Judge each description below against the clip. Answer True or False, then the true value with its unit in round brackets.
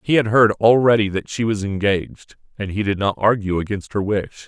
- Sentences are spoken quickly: True (215 wpm)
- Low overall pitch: True (105 Hz)